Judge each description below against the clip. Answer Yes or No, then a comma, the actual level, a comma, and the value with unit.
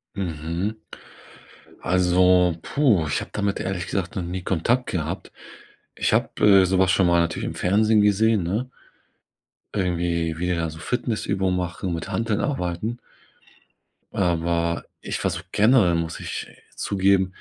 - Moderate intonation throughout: Yes, average, 3.3 semitones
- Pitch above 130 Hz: No, very low, 90 Hz